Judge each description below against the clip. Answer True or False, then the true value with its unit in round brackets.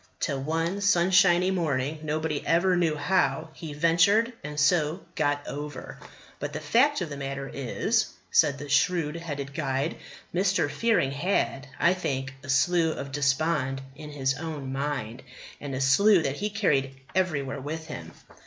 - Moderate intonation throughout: True (4.0 semitones)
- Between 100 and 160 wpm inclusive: True (155 wpm)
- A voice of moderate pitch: True (150 Hz)